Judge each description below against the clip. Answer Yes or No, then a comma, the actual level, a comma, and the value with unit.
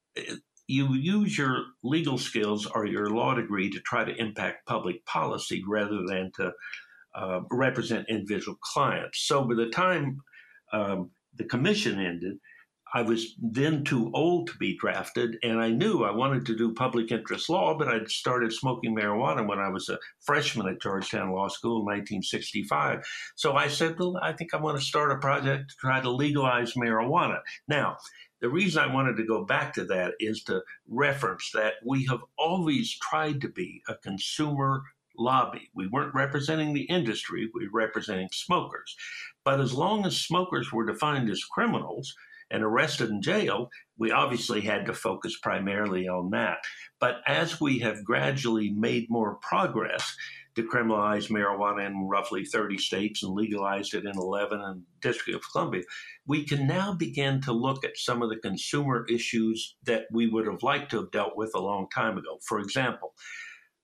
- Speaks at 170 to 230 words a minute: Yes, average, 175 wpm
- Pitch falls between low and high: No, low, 115 Hz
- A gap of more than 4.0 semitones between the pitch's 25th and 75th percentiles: Yes, average, 4.8 semitones